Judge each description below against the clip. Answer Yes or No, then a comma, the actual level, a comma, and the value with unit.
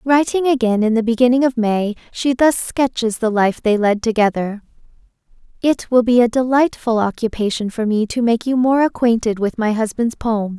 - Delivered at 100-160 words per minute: No, average, 180 wpm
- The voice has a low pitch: No, high, 235 Hz